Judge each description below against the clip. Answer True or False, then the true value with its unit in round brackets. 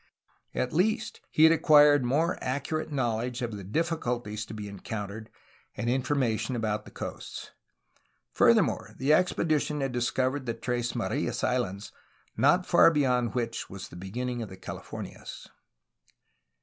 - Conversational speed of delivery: True (150 wpm)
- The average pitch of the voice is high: False (125 Hz)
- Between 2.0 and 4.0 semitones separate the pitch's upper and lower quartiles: False (4.8 semitones)